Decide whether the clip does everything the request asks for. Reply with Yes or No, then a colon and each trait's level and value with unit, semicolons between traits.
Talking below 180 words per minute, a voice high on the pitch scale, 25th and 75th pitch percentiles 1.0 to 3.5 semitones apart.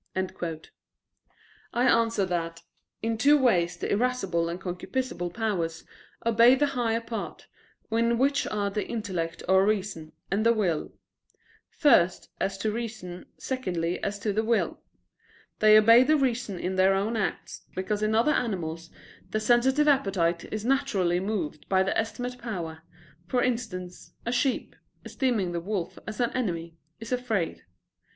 No: average, 145 wpm; high, 215 Hz; average, 4.8 semitones